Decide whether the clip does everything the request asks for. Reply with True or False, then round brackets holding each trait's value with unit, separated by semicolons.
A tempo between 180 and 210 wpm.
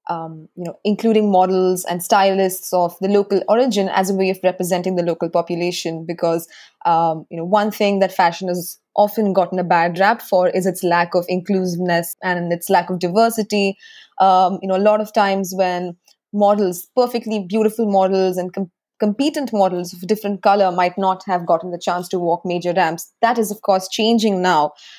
True (190 wpm)